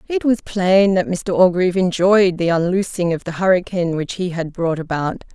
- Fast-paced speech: No, average, 190 wpm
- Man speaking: No, female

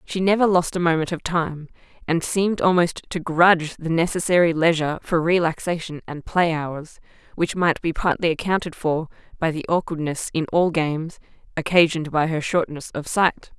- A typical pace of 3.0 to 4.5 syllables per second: No, 5.2 syllables/s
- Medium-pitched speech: Yes, medium, 165 Hz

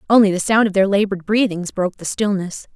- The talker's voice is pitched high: Yes, high, 200 Hz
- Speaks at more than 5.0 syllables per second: Yes, 6.4 syllables/s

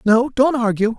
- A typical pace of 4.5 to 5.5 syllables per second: Yes, 4.6 syllables/s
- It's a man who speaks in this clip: Yes, male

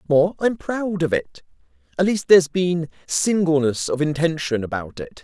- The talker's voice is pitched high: No, medium, 155 Hz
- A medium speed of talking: Yes, average, 160 wpm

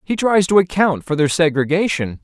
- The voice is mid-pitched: Yes, medium, 170 Hz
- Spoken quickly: No, average, 190 wpm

